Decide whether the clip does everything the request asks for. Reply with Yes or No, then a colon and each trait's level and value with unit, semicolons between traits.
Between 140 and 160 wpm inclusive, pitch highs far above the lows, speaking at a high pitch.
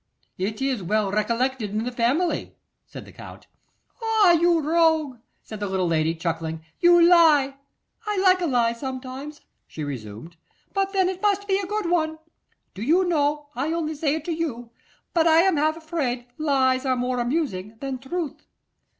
No: average, 175 wpm; wide, 6.5 semitones; very high, 285 Hz